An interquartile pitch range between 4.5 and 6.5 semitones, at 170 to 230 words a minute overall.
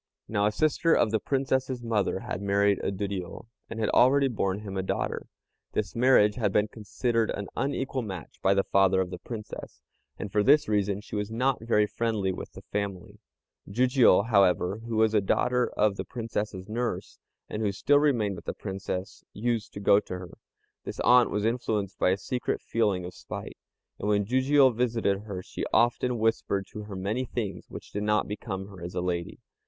No: average, 3.3 semitones; average, 195 wpm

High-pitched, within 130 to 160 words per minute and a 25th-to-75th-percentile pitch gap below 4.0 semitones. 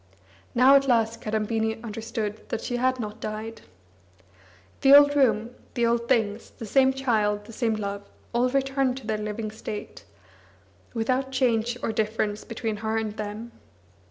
Yes: high, 225 Hz; average, 155 wpm; average, 2.9 semitones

